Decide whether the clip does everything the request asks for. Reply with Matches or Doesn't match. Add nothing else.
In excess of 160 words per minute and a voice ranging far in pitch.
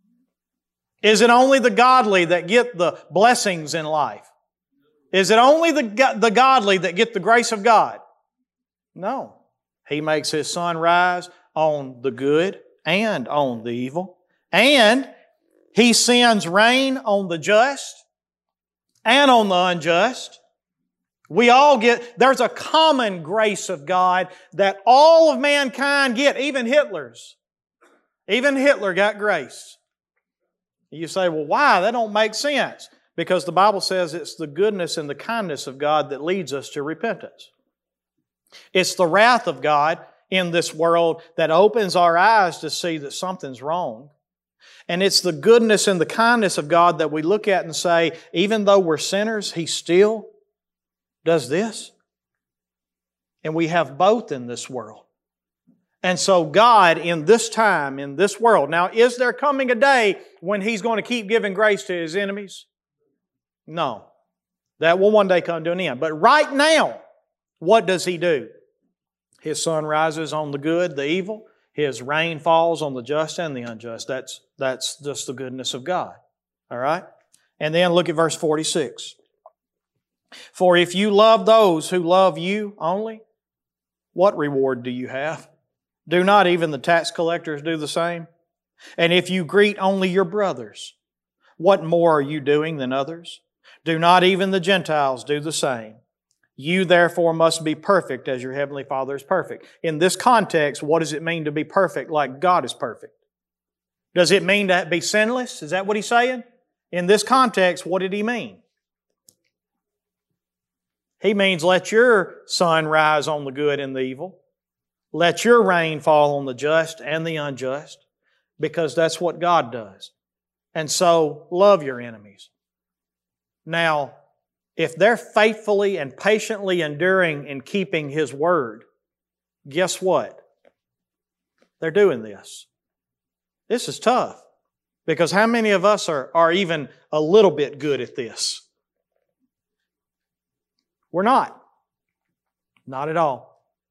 Doesn't match